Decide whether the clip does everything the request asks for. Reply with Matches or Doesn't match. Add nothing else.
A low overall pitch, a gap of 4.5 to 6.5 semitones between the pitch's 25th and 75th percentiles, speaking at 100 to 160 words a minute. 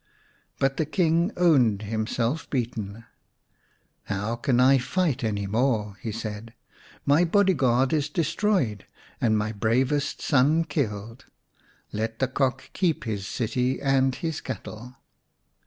Matches